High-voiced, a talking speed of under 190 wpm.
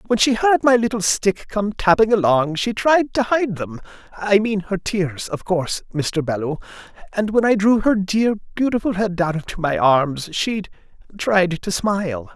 Yes: high, 195 Hz; average, 175 wpm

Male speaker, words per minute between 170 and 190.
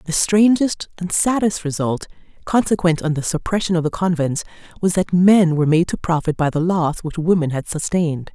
No: female; average, 185 wpm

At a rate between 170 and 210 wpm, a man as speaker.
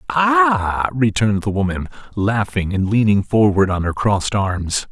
No: average, 145 wpm; male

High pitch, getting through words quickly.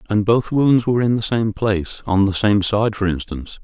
No: low, 105 Hz; fast, 215 wpm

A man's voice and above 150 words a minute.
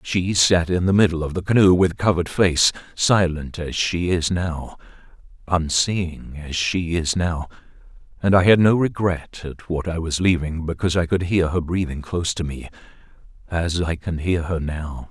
Yes: male; average, 175 wpm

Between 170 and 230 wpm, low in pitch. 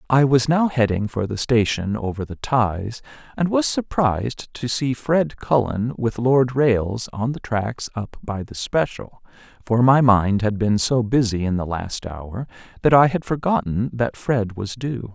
Yes: average, 180 wpm; low, 120 Hz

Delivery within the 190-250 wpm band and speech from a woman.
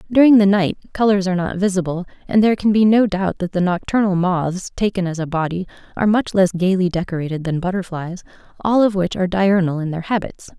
Yes: fast, 205 wpm; female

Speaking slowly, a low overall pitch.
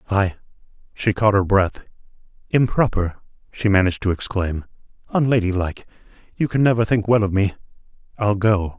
Yes: slow, 115 wpm; low, 100 Hz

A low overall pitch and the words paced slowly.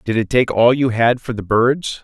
No: low, 120 Hz; fast, 265 wpm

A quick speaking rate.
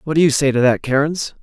Yes: fast, 295 wpm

